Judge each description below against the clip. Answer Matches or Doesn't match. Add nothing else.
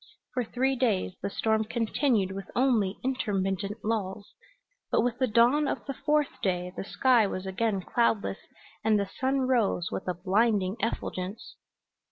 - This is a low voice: Doesn't match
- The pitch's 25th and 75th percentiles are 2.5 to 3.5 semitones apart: Doesn't match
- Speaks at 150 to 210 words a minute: Matches